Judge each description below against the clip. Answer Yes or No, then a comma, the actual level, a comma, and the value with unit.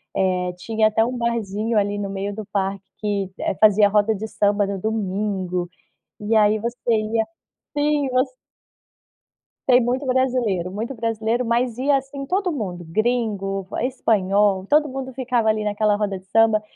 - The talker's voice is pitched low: No, high, 215 Hz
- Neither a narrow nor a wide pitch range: Yes, average, 3.5 semitones